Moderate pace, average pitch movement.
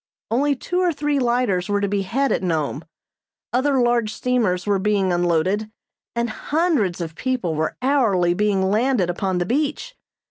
No: average, 165 wpm; wide, 6.0 semitones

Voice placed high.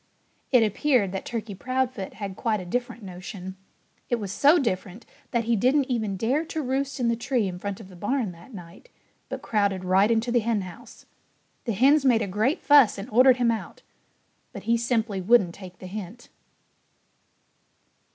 Yes: high, 225 Hz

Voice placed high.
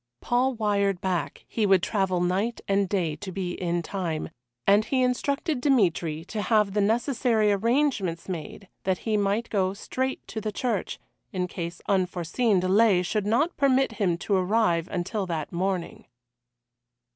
Yes: high, 200 Hz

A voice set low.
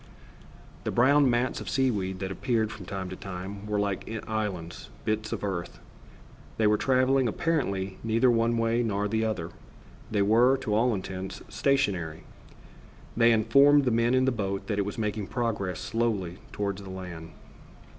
Yes: low, 110 Hz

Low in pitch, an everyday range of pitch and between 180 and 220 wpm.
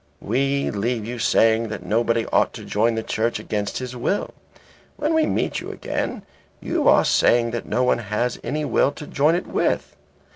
Yes: low, 120 Hz; average, 3.6 semitones; average, 185 wpm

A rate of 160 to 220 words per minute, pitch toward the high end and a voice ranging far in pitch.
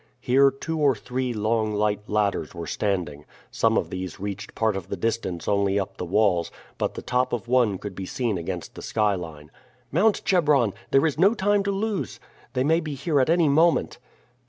No: average, 195 wpm; low, 110 Hz; wide, 6.5 semitones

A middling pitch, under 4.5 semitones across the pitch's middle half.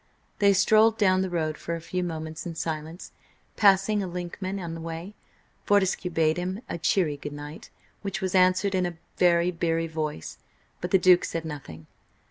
Yes: medium, 175 Hz; average, 2.7 semitones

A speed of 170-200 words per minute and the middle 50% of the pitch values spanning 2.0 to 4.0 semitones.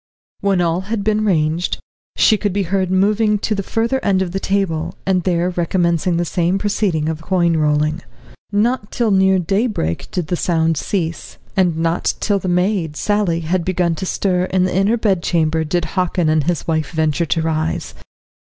Yes: average, 180 wpm; average, 3.2 semitones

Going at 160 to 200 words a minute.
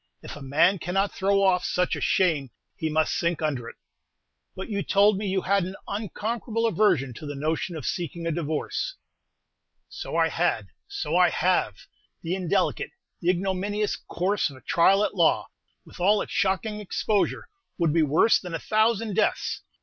Yes: average, 175 wpm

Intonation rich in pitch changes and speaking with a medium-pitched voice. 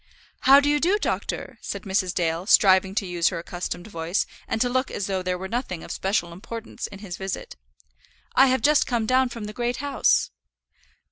No: wide, 5.7 semitones; high, 205 Hz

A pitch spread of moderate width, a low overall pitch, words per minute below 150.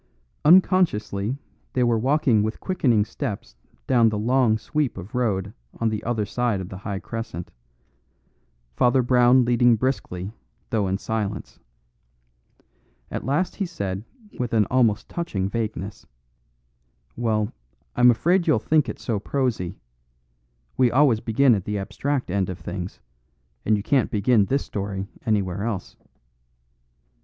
Yes: average, 4.1 semitones; low, 115 Hz; slow, 135 wpm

